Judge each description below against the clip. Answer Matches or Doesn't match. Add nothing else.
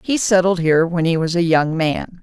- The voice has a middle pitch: Matches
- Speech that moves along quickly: Matches